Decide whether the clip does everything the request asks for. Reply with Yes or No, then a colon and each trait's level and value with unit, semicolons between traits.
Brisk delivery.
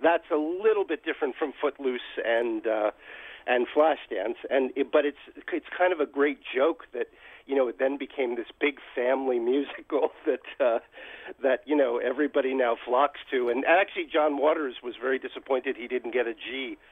No: average, 180 wpm